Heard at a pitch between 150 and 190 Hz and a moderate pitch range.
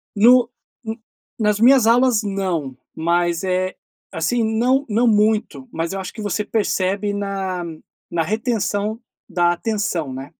No: high, 205 Hz; average, 4.0 semitones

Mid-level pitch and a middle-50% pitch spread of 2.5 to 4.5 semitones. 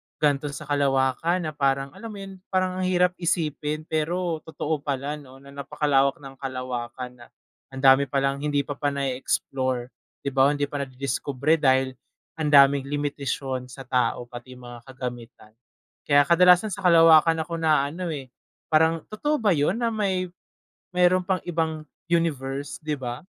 Yes: medium, 145 Hz; average, 3.8 semitones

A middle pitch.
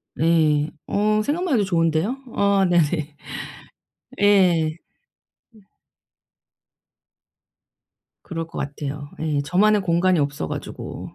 Yes: medium, 170 Hz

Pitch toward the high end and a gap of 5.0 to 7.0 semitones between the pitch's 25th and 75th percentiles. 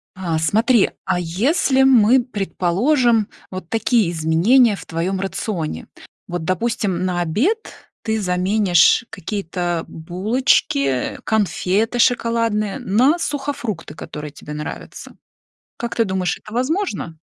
Yes: high, 200 Hz; average, 5.3 semitones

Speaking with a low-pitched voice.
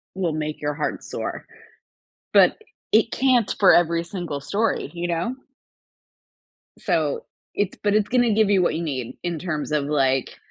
No: medium, 175 Hz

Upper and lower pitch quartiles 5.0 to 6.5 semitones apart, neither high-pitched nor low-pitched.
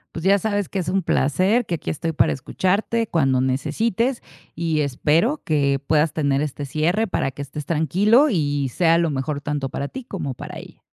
Yes: wide, 5.5 semitones; medium, 160 Hz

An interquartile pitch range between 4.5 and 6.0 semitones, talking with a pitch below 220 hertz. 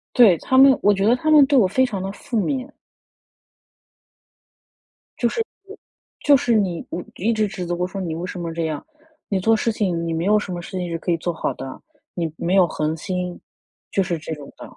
Yes: average, 5.1 semitones; high, 190 Hz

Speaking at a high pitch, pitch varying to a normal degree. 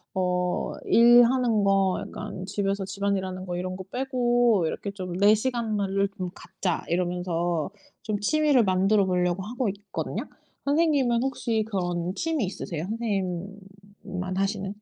Yes: high, 200 Hz; average, 4.0 semitones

